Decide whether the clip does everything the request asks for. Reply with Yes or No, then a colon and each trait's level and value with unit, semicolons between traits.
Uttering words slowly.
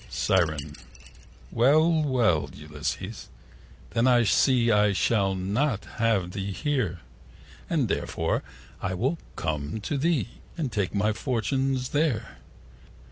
Yes: slow, 115 wpm